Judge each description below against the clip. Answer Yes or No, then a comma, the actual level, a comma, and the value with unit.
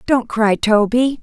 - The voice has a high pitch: Yes, high, 230 Hz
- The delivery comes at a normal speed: Yes, average, 145 wpm